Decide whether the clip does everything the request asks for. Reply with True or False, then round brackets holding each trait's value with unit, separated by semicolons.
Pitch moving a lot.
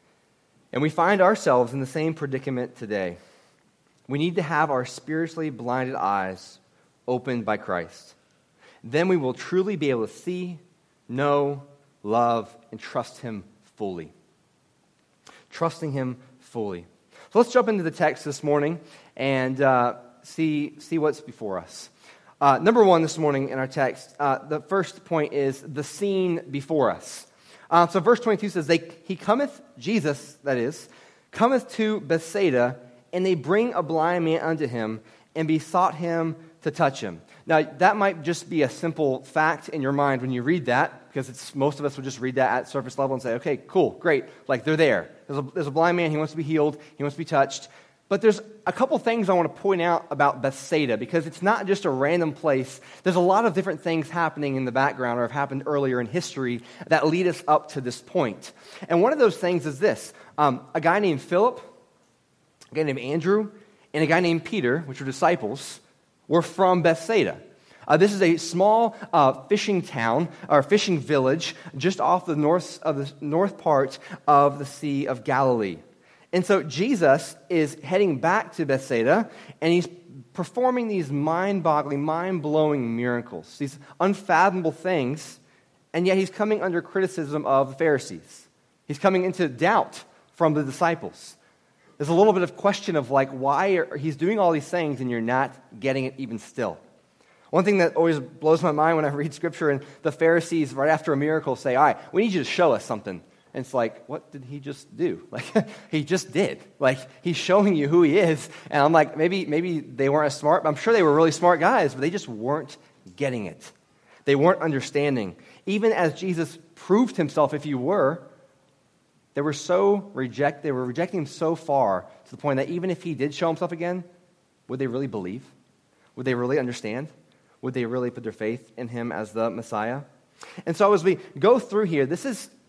False (4.6 semitones)